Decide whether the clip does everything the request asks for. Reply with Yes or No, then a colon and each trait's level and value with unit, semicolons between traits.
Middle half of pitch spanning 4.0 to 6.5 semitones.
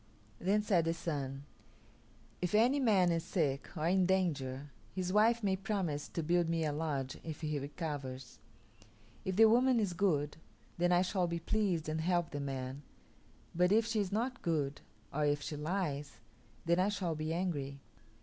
Yes: average, 4.5 semitones